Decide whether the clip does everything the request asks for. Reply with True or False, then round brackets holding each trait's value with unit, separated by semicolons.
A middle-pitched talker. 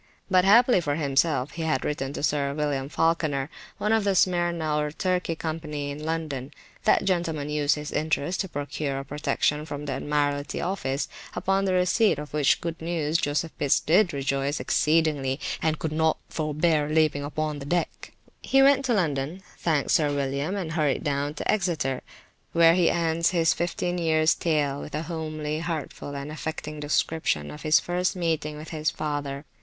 True (155 Hz)